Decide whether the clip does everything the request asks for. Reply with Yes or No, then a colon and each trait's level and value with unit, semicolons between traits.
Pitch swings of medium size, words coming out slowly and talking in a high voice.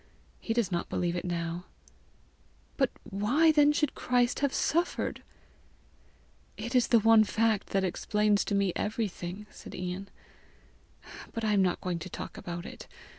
No: average, 4.7 semitones; average, 160 wpm; high, 210 Hz